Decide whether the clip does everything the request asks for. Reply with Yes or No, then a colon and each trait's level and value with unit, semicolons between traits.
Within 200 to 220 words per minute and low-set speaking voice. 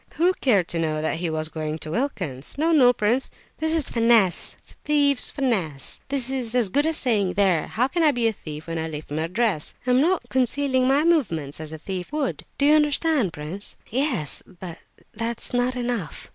No: fast, 205 wpm; high, 230 Hz